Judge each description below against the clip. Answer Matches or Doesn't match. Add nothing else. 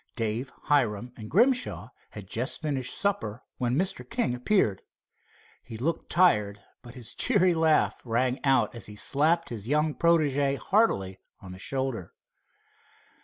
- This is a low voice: Matches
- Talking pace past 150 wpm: Doesn't match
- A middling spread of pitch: Doesn't match